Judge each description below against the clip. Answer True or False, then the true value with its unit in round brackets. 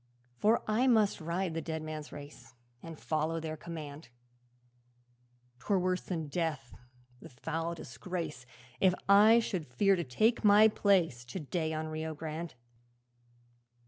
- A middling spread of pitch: True (3.7 semitones)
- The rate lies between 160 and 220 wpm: False (140 wpm)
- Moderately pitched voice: True (165 Hz)